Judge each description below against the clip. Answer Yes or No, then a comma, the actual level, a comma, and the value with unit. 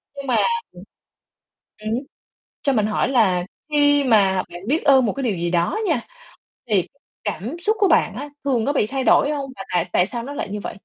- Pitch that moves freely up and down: Yes, wide, 5.8 semitones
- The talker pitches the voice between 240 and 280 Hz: Yes, high, 245 Hz